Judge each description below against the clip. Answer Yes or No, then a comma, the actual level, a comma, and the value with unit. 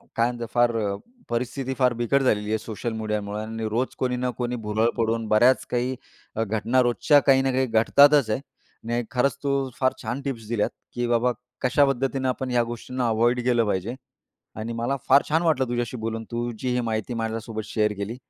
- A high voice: No, low, 120 Hz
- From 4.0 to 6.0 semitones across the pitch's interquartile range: No, narrow, 2.4 semitones